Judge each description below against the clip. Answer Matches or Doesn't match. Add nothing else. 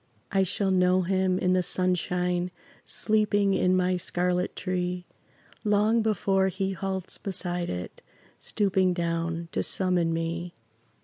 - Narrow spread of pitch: Matches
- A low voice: Doesn't match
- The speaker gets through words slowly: Matches